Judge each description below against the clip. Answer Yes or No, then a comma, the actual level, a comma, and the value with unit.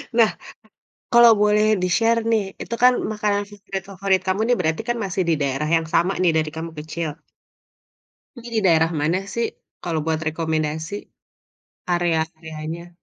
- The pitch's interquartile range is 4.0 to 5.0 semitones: Yes, average, 4.6 semitones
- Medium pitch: Yes, medium, 175 Hz